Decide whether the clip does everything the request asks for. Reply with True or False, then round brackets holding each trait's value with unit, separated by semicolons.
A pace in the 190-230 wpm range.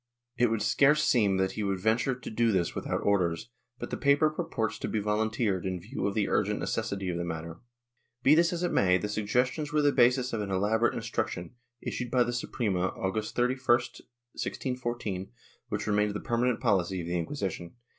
True (195 wpm)